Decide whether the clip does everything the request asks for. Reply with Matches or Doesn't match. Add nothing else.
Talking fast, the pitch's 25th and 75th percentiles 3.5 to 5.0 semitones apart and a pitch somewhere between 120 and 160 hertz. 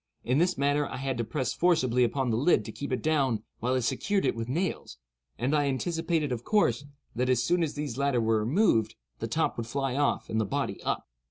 Matches